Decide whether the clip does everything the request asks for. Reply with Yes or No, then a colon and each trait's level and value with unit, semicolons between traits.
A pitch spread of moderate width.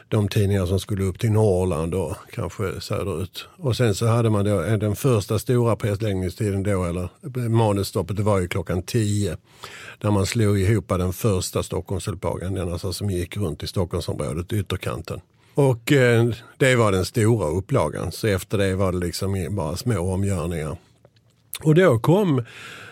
Yes: average, 3.7 semitones